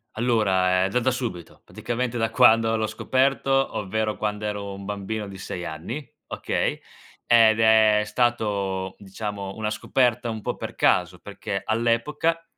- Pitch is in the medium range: No, low, 110 Hz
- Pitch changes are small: No, average, 3.2 semitones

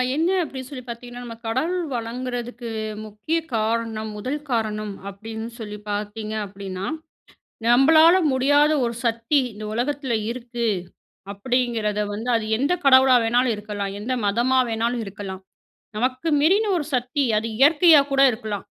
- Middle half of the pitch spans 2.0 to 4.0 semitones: Yes, average, 3.4 semitones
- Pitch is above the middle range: Yes, high, 235 Hz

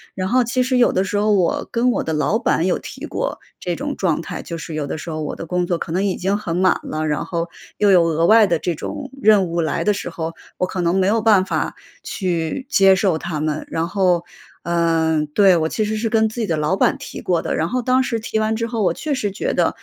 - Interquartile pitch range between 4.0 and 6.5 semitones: Yes, average, 4.6 semitones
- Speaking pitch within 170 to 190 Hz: Yes, medium, 185 Hz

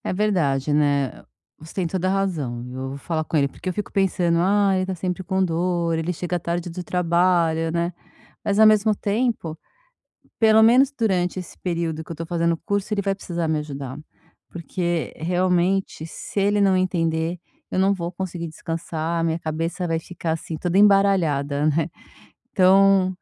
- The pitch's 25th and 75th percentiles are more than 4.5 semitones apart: No, average, 2.9 semitones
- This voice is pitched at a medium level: Yes, medium, 175 Hz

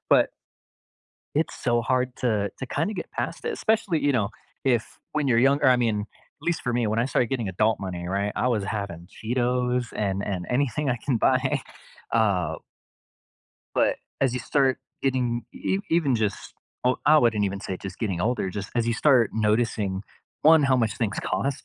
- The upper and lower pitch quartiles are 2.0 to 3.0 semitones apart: No, average, 4.1 semitones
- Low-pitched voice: Yes, low, 120 Hz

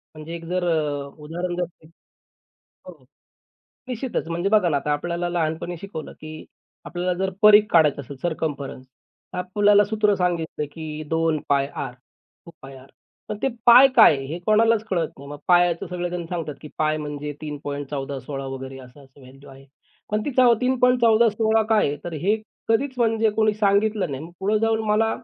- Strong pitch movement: Yes, wide, 6.1 semitones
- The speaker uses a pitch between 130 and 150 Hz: No, medium, 170 Hz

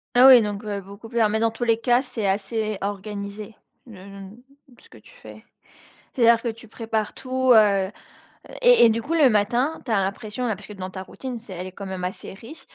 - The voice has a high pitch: Yes, high, 220 Hz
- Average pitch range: Yes, average, 3.1 semitones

